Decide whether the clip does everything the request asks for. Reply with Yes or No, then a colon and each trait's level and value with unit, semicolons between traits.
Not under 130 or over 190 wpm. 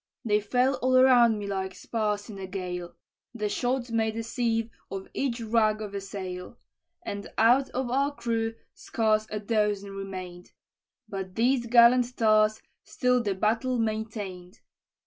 Yes: average, 150 wpm